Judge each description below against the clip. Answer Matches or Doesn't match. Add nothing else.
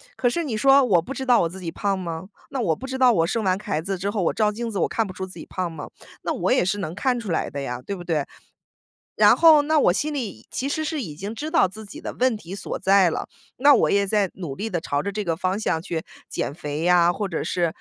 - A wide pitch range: Matches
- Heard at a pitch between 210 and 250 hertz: Doesn't match